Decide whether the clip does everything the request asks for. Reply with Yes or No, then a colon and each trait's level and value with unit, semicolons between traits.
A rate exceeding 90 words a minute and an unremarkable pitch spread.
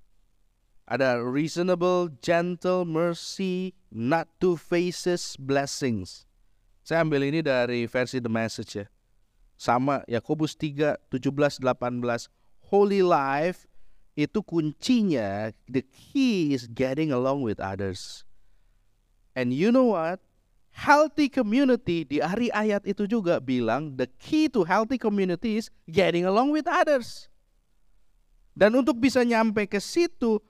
No: average, 120 wpm; wide, 8.7 semitones